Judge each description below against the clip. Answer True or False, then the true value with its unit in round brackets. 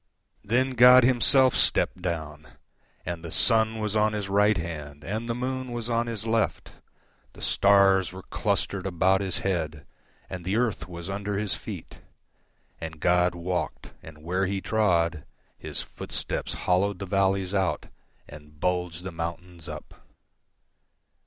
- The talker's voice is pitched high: False (95 Hz)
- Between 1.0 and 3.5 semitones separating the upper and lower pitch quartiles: False (4.1 semitones)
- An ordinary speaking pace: False (125 wpm)